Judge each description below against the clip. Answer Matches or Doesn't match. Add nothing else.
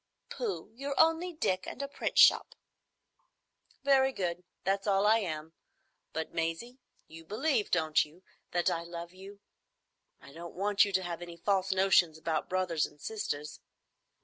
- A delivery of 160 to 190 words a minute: Doesn't match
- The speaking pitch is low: Doesn't match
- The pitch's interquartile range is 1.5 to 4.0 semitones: Doesn't match